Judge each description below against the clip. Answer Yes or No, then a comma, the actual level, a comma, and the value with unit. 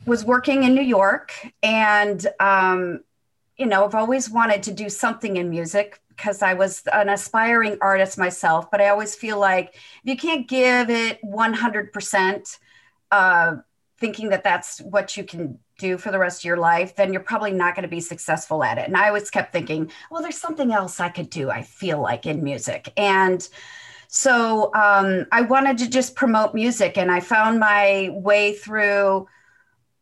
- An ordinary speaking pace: Yes, average, 180 wpm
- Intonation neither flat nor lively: Yes, average, 3.5 semitones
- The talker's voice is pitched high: Yes, high, 205 Hz